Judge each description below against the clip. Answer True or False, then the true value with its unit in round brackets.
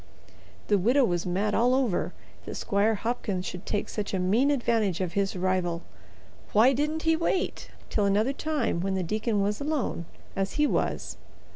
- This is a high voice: True (210 Hz)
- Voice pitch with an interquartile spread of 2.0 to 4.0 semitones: False (5.3 semitones)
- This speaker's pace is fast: False (170 wpm)